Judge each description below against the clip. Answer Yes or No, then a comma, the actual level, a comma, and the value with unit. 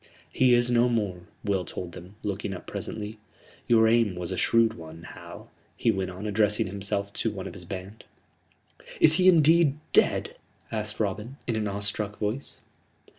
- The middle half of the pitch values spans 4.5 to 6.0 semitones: No, average, 3.2 semitones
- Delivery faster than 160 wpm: Yes, average, 170 wpm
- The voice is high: No, low, 105 Hz